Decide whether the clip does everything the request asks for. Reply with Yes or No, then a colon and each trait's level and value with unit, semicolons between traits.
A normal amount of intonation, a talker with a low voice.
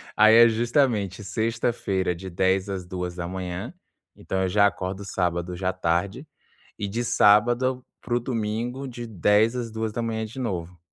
Yes: average, 3.9 semitones; low, 105 Hz